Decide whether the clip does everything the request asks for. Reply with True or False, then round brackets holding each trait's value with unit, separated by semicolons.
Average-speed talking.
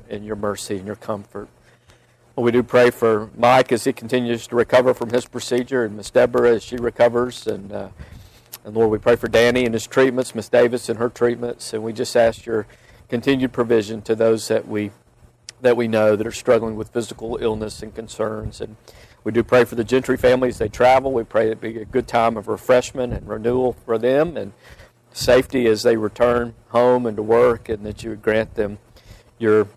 False (210 wpm)